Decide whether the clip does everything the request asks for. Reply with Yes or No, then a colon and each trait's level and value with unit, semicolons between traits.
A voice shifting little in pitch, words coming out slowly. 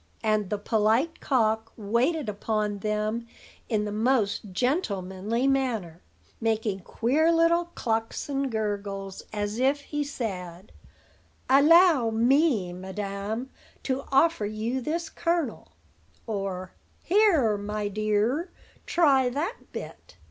No: average, 4.9 semitones; slow, 110 wpm